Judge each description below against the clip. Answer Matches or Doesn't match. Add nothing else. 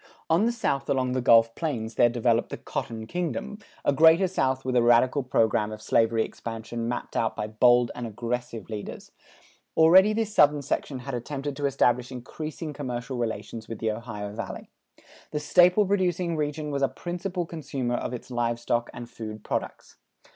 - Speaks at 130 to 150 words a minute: Doesn't match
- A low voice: Matches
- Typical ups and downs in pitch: Matches